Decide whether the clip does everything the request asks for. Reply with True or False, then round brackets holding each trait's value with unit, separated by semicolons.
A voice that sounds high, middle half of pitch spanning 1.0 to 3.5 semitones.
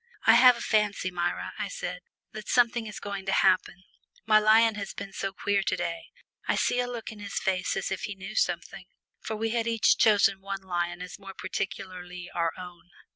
True (200 Hz; 3.0 semitones)